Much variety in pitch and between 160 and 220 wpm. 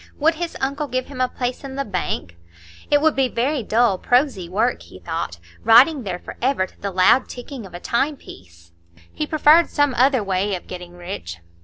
Yes: wide, 7.0 semitones; average, 190 wpm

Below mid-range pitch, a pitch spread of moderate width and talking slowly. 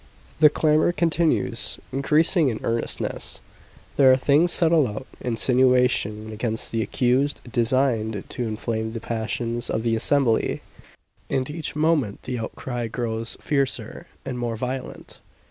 Yes: low, 125 Hz; average, 3.9 semitones; slow, 130 wpm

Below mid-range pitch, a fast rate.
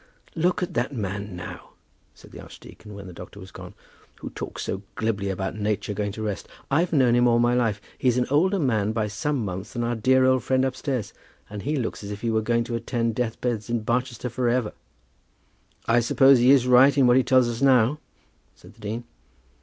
Yes: low, 120 Hz; fast, 215 wpm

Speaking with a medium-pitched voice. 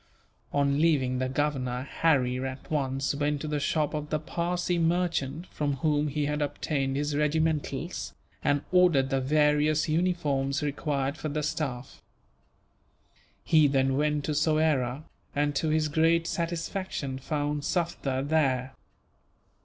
Yes: medium, 150 Hz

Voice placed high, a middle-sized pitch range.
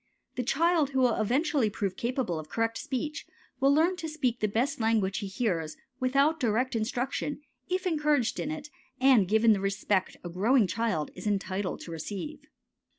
No: high, 240 Hz; wide, 5.8 semitones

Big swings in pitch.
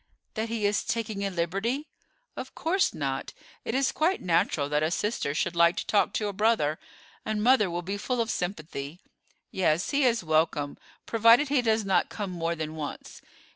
Yes: wide, 5.7 semitones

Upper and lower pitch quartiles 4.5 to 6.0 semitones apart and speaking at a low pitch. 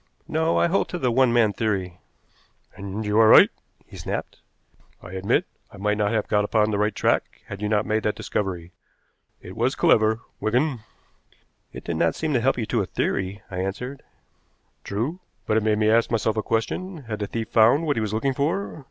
No: average, 3.3 semitones; low, 110 Hz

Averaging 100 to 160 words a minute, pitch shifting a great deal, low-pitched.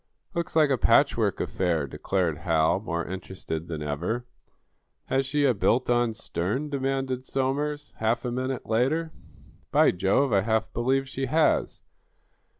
Yes: average, 145 wpm; wide, 6.3 semitones; low, 120 Hz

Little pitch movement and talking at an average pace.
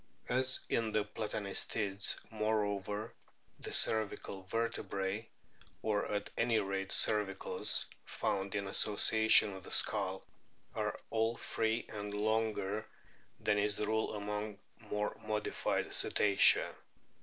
No: narrow, 1.5 semitones; slow, 110 wpm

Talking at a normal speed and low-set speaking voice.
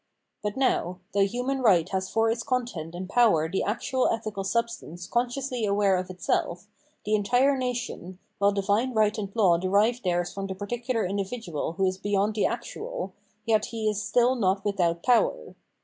No: average, 170 wpm; high, 205 Hz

